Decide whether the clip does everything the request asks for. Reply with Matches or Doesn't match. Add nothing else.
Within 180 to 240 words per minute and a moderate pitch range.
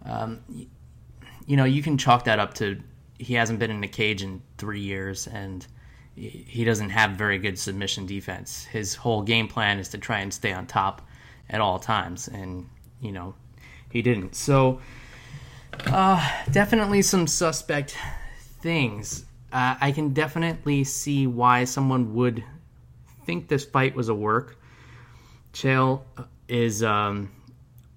Doesn't match